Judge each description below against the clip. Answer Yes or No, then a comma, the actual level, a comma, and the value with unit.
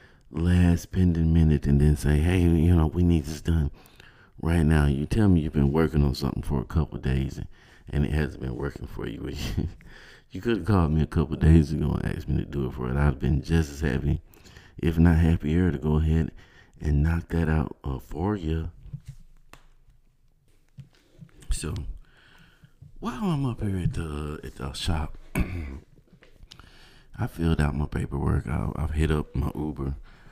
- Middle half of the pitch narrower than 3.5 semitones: Yes, average, 2.9 semitones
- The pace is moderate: Yes, average, 185 wpm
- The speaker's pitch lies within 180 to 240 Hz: No, very low, 80 Hz